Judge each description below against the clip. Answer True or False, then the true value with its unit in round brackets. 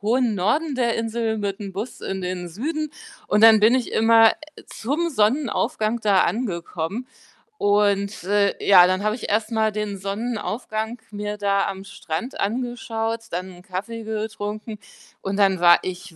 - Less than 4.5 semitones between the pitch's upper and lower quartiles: True (2.6 semitones)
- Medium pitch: False (210 Hz)